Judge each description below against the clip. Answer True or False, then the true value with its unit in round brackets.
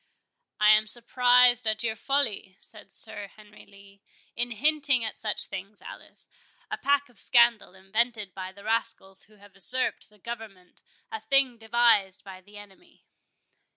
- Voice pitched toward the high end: True (220 Hz)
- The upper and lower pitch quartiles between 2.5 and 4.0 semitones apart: True (3.3 semitones)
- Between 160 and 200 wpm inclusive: False (150 wpm)